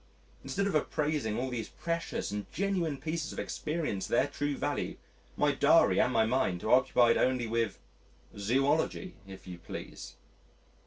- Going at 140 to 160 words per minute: Yes, average, 155 wpm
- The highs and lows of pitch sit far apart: Yes, wide, 5.9 semitones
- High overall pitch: No, low, 130 Hz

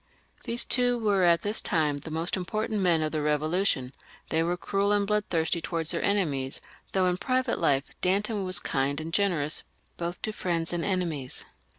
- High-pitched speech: No, medium, 175 Hz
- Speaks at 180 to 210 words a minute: Yes, average, 185 wpm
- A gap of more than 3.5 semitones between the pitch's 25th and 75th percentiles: Yes, average, 4.4 semitones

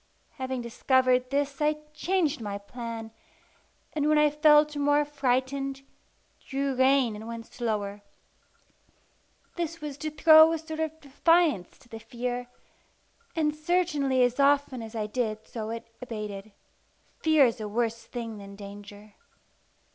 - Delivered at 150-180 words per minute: No, average, 140 wpm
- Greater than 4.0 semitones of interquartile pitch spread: Yes, average, 4.9 semitones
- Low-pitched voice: No, very high, 260 Hz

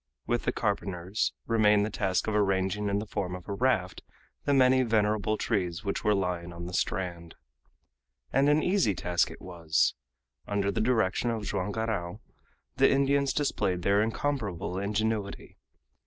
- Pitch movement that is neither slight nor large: Yes, average, 3.6 semitones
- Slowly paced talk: No, average, 155 wpm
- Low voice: Yes, low, 105 Hz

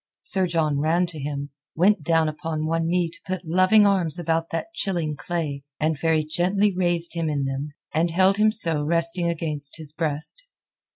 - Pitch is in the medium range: Yes, medium, 165 Hz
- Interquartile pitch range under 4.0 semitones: Yes, narrow, 2.6 semitones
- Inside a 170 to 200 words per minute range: Yes, average, 180 wpm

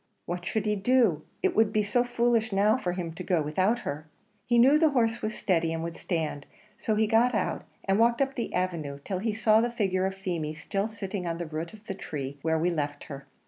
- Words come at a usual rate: No, fast, 235 wpm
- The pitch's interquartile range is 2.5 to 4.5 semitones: No, average, 5.2 semitones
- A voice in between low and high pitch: No, high, 195 Hz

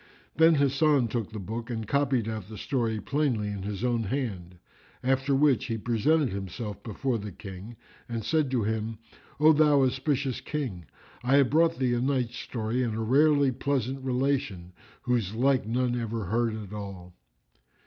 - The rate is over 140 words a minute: Yes, average, 170 wpm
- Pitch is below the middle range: Yes, low, 120 Hz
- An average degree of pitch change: Yes, average, 4.1 semitones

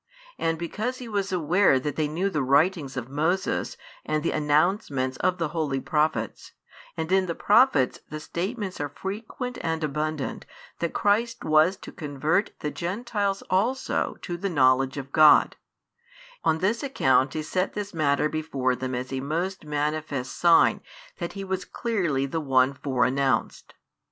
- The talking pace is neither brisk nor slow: Yes, average, 160 wpm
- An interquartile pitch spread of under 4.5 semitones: No, average, 5.3 semitones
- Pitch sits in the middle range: Yes, medium, 155 Hz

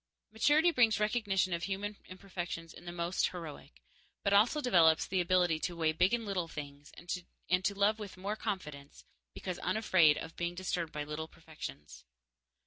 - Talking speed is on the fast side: No, average, 165 wpm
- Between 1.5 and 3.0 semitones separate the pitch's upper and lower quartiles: No, average, 4.0 semitones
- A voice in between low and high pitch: Yes, medium, 180 Hz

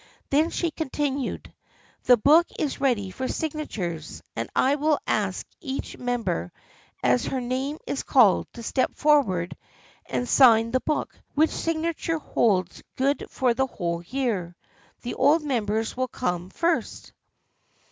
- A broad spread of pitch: Yes, wide, 6.1 semitones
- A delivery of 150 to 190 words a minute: No, average, 140 wpm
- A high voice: Yes, very high, 255 Hz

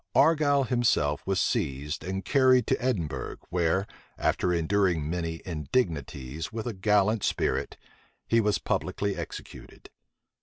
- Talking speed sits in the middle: No, slow, 120 wpm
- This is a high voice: No, very low, 95 Hz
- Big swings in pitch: Yes, wide, 6.0 semitones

